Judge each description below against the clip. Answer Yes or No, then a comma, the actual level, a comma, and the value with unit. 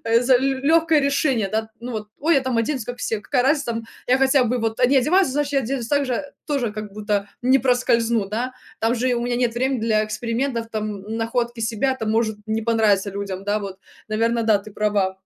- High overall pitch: Yes, high, 230 Hz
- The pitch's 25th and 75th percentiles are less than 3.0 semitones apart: No, average, 3.3 semitones